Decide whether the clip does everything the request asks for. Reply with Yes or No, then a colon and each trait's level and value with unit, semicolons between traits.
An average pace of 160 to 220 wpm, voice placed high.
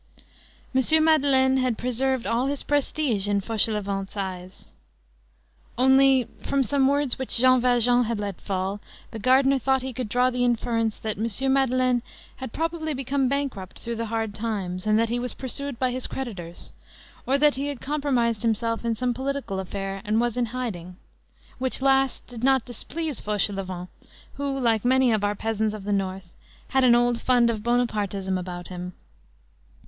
Yes: average, 170 wpm; high, 240 Hz